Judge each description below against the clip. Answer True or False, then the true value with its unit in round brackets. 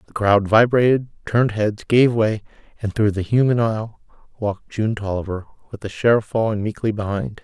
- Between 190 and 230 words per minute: False (170 wpm)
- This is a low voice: True (110 Hz)